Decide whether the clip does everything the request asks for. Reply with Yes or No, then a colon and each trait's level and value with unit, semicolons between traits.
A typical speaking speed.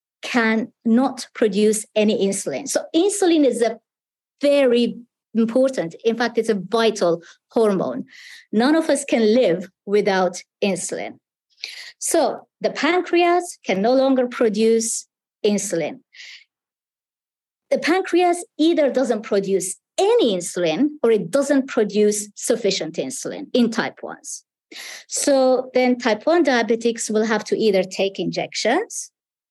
No: slow, 120 wpm